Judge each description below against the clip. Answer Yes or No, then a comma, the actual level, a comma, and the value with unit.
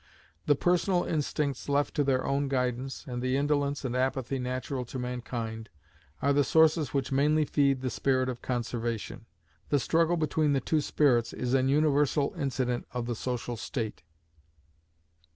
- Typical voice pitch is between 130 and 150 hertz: Yes, low, 135 Hz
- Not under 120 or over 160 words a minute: Yes, average, 155 wpm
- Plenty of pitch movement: No, narrow, 2.6 semitones